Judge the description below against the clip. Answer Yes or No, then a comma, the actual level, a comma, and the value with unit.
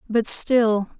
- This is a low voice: No, high, 225 Hz